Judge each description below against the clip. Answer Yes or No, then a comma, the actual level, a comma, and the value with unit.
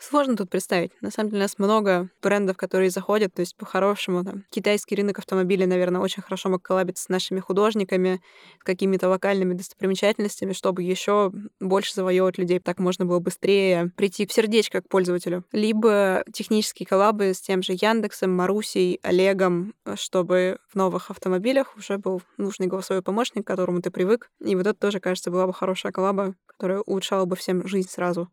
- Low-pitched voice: No, high, 190 Hz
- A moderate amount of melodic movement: No, narrow, 1.7 semitones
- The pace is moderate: No, fast, 175 wpm